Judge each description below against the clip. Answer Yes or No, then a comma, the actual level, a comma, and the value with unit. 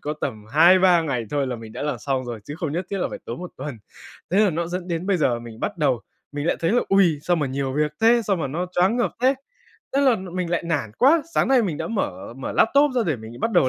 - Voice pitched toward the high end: No, medium, 165 Hz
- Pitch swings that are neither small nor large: No, wide, 5.8 semitones